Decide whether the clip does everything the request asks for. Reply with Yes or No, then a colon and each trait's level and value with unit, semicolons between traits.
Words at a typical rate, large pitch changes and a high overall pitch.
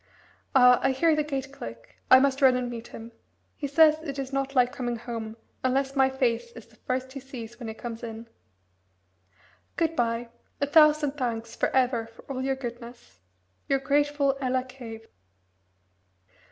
No: average, 170 wpm; average, 2.7 semitones; very high, 255 Hz